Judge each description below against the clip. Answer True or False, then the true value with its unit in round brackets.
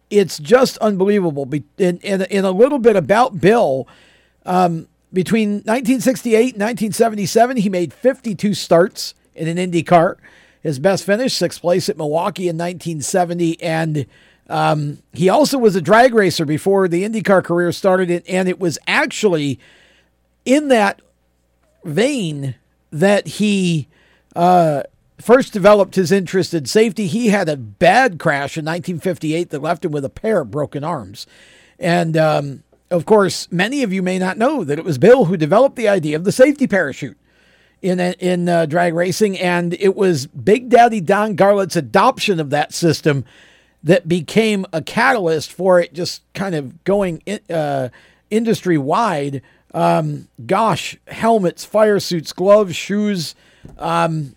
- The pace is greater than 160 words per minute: False (150 wpm)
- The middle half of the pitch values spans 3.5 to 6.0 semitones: True (4.2 semitones)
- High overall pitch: False (180 Hz)